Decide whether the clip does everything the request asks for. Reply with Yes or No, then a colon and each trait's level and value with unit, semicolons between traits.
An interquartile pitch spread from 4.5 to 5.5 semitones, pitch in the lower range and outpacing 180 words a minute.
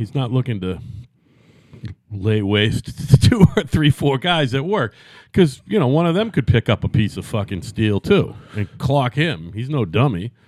Yes: average, 5.0 semitones; low, 125 Hz; average, 200 wpm